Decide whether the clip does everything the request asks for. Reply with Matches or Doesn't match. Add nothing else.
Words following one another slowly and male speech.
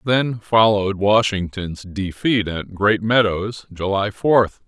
Matches